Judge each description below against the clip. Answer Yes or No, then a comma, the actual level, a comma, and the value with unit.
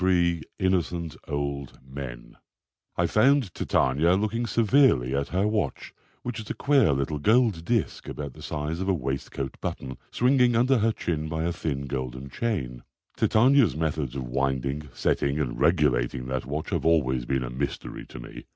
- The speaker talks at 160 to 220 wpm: Yes, average, 165 wpm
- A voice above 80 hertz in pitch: No, very low, 75 Hz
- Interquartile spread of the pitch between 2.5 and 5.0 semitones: No, wide, 7.8 semitones